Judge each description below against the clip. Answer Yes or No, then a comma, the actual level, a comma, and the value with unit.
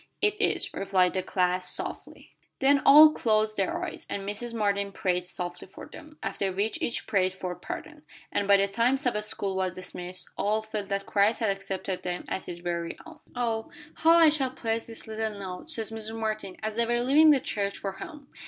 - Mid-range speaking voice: No, high, 210 Hz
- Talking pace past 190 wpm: Yes, average, 200 wpm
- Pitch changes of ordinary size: Yes, average, 3.7 semitones